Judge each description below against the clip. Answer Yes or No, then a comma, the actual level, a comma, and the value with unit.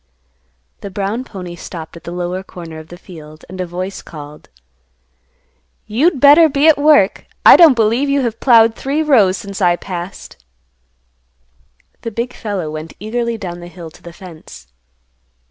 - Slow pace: No, average, 160 wpm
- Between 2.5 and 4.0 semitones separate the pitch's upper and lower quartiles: No, wide, 5.6 semitones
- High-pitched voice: Yes, high, 195 Hz